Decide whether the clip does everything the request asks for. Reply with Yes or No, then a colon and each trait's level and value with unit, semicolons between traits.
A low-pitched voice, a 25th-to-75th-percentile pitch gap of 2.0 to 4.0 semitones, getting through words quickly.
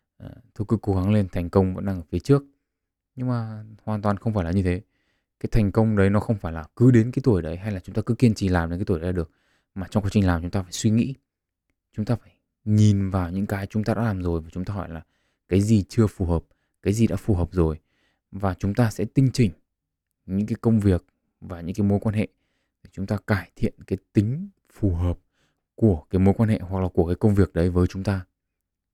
Yes: low, 100 Hz; average, 3.3 semitones; fast, 260 wpm